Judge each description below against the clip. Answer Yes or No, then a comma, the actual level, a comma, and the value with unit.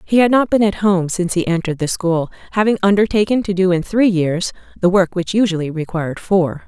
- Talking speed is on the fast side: Yes, fast, 215 wpm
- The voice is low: No, medium, 185 Hz